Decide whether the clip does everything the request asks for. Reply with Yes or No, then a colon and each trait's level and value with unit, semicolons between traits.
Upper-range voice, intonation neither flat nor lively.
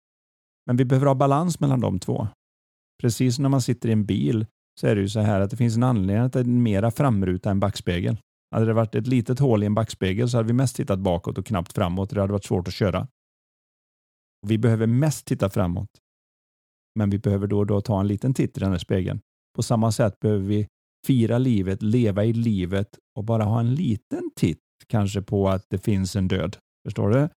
No: low, 110 Hz; average, 3.7 semitones